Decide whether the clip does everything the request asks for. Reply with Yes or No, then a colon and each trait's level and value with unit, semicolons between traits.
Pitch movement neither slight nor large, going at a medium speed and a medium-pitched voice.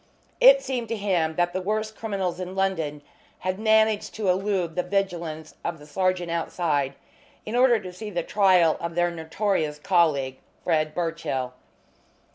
Yes: average, 4.0 semitones; average, 155 wpm; medium, 180 Hz